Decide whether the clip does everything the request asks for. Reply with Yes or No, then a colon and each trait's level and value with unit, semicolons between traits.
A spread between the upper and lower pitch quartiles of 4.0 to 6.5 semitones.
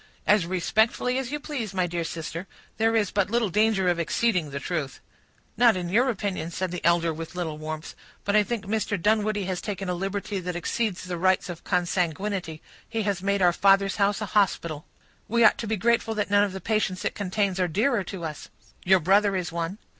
No: average, 3.4 semitones